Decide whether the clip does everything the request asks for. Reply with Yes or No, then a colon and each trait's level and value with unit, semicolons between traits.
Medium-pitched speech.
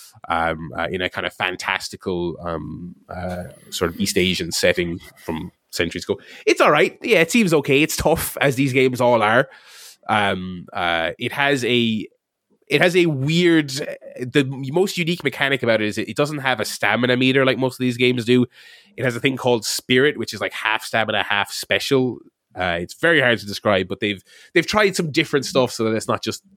No: low, 125 Hz